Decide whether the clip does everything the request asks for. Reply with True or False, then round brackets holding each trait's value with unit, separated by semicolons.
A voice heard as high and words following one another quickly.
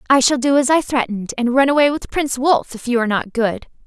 True (255 Hz; 265 wpm)